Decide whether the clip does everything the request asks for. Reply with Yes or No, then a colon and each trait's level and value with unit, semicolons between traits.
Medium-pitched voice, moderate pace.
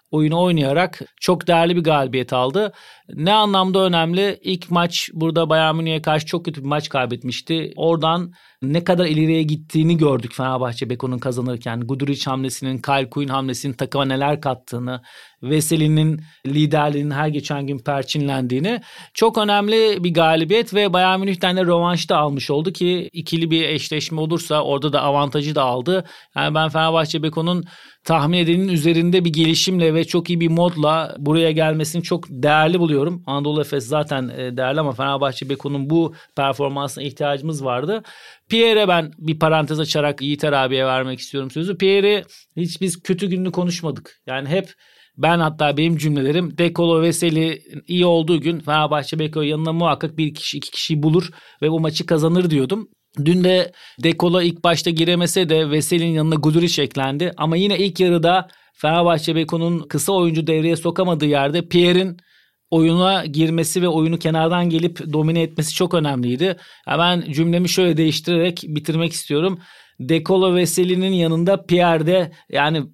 No: medium, 160 Hz; fast, 150 wpm